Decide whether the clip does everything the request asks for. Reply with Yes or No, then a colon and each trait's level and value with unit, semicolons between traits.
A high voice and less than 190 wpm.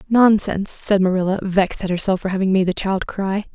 No: high, 195 Hz; fast, 205 wpm